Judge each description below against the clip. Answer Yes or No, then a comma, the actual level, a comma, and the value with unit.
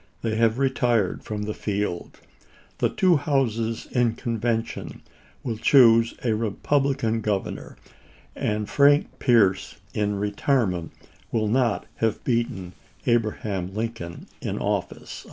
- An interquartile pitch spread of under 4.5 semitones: Yes, average, 2.7 semitones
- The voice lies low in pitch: Yes, low, 115 Hz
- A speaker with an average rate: No, slow, 115 wpm